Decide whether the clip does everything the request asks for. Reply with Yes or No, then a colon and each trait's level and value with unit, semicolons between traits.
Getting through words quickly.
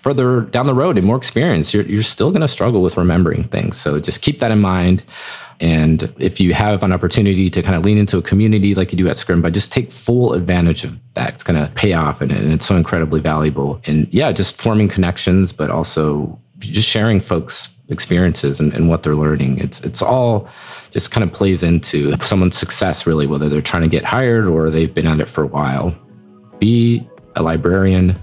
Yes: fast, 215 wpm